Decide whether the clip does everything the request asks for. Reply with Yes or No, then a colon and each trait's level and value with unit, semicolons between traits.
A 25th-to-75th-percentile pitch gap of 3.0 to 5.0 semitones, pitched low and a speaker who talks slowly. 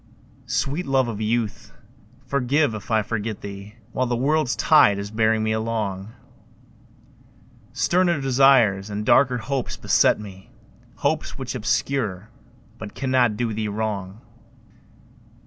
Yes: average, 3.8 semitones; low, 110 Hz; slow, 125 wpm